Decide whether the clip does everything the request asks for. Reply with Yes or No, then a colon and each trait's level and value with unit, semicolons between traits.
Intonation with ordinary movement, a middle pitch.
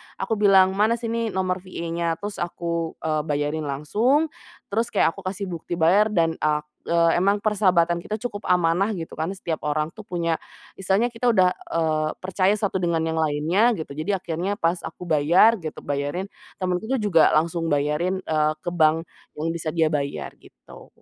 Yes: average, 3.8 semitones; medium, 170 Hz